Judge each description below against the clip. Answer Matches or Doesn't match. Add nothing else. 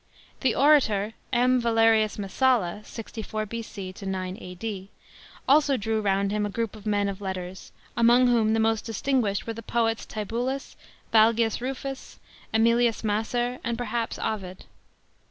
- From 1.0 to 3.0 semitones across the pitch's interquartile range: Matches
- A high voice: Matches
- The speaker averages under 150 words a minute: Matches